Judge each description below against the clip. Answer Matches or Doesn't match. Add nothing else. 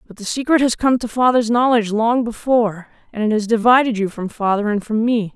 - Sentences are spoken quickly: Matches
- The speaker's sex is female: Matches